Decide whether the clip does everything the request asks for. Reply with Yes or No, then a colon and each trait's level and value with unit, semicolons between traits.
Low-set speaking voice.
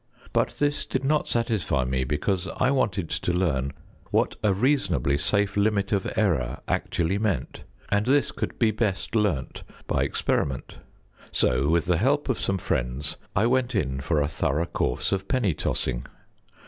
Yes: very low, 95 Hz